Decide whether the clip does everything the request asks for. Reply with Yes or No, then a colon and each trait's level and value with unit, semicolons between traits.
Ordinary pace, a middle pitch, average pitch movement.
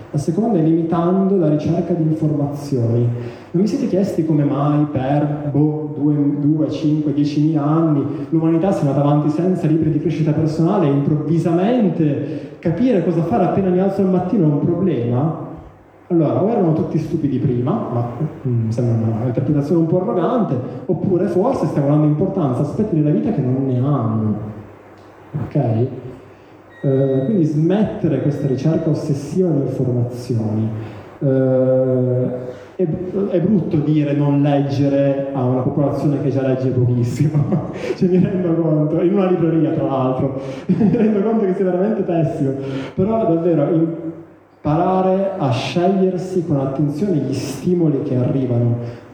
Yes: average, 150 wpm; medium, 150 Hz; average, 4.3 semitones